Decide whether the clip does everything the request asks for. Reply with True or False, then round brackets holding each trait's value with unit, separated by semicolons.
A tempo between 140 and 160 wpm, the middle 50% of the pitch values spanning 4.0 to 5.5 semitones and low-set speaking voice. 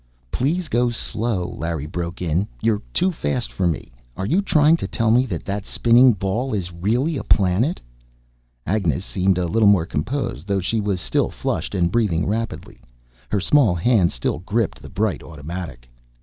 False (175 wpm; 5.2 semitones; 100 Hz)